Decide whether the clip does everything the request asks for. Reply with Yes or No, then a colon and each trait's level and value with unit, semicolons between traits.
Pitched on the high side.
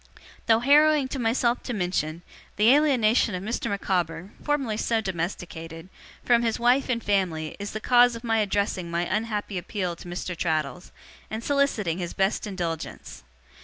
Yes: high, 205 Hz